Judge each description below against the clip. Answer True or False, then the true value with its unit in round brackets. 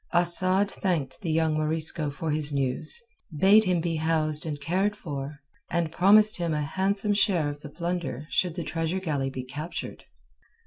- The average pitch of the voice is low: False (165 Hz)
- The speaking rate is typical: True (170 wpm)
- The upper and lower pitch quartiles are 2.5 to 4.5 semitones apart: True (3.7 semitones)